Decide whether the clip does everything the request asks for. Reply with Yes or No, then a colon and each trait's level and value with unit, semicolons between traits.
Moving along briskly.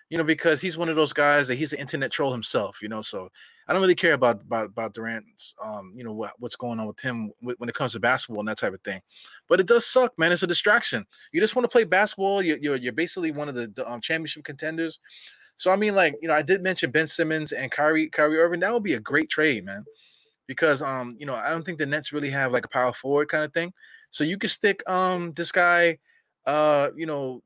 Yes: fast, 260 wpm